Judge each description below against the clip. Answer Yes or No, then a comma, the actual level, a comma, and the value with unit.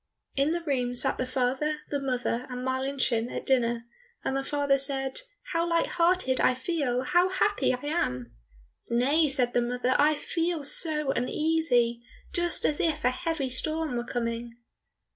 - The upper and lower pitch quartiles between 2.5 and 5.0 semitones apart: Yes, average, 3.9 semitones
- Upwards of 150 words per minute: Yes, average, 160 wpm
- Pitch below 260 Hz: No, very high, 270 Hz